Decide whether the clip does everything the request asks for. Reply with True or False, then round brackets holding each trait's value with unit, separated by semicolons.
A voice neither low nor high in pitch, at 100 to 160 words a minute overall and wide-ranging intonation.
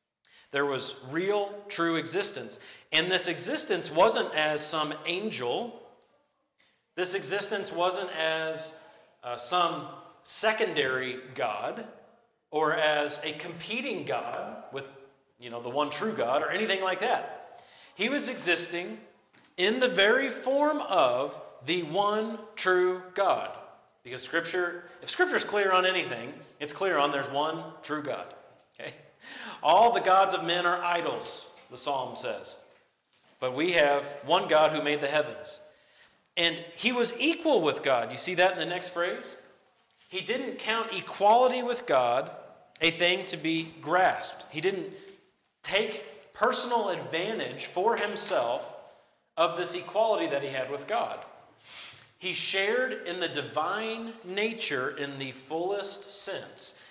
True (180 Hz; 140 wpm; 6.3 semitones)